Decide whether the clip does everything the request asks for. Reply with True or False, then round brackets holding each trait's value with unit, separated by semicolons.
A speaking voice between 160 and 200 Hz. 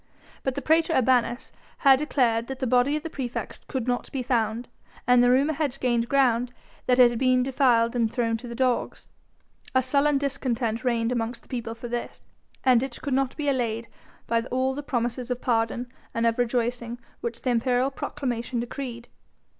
False (245 Hz)